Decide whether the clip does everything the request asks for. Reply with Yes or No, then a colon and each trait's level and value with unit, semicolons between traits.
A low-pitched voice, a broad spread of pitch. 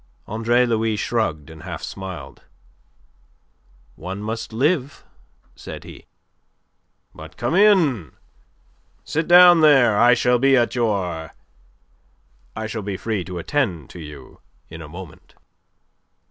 Yes: low, 110 Hz; wide, 6.3 semitones